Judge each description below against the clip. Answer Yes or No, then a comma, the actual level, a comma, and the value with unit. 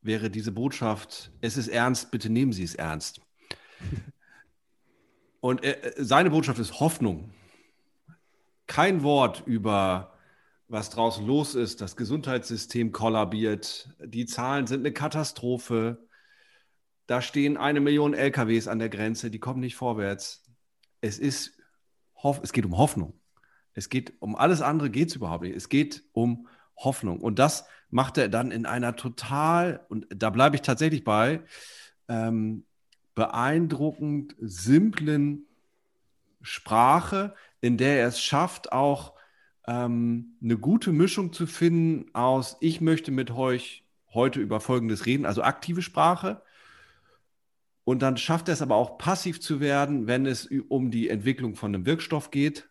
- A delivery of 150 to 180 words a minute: No, average, 140 wpm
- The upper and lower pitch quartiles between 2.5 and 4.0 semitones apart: No, average, 4.4 semitones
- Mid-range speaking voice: No, low, 125 Hz